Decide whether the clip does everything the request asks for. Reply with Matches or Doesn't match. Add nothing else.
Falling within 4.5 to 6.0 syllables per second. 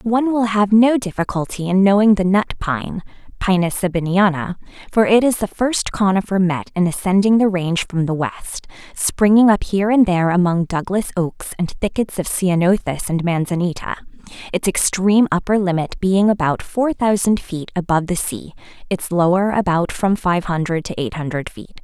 Matches